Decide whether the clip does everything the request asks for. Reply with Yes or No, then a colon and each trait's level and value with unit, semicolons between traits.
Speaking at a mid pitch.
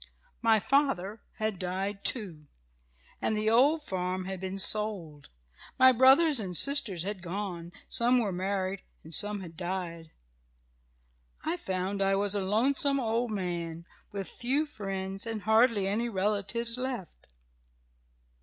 No: high, 200 Hz